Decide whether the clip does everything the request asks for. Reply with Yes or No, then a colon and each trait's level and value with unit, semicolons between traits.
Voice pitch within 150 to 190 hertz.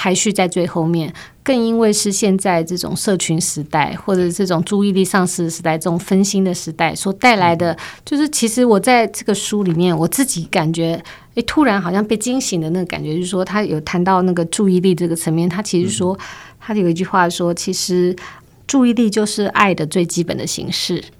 Yes: medium, 185 Hz